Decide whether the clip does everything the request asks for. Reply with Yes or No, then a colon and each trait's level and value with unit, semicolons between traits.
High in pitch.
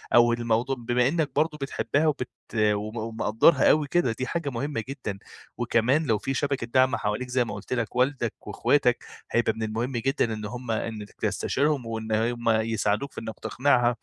No: low, 120 Hz